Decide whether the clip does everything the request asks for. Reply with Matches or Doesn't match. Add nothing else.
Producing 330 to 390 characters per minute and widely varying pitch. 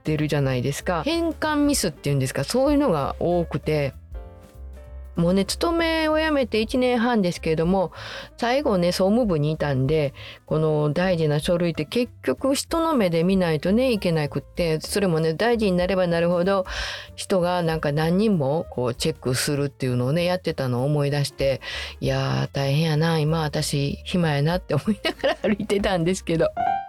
Matches